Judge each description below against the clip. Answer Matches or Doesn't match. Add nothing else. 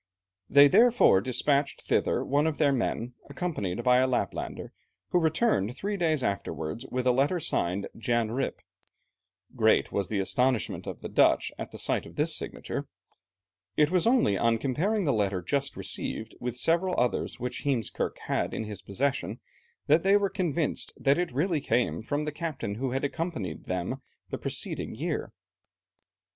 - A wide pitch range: Matches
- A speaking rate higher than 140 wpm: Matches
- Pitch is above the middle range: Doesn't match